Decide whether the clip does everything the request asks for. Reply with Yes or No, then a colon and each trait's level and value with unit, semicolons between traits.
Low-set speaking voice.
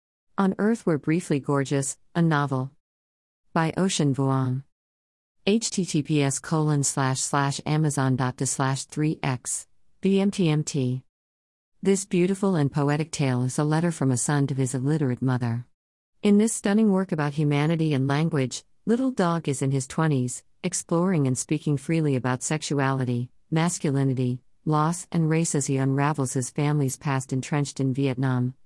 No: medium, 145 Hz